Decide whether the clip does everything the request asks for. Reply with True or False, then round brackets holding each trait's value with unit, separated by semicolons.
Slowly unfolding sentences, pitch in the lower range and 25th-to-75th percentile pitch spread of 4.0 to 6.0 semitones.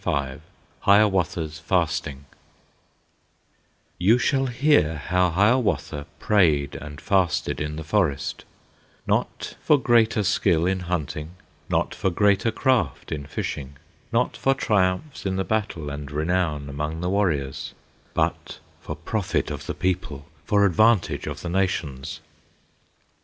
True (125 wpm; 90 Hz; 5.5 semitones)